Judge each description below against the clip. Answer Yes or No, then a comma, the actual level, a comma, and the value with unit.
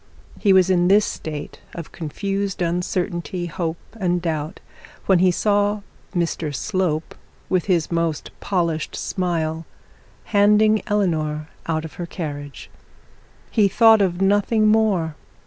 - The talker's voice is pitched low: No, medium, 180 Hz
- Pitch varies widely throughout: No, average, 3.8 semitones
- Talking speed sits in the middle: No, slow, 125 wpm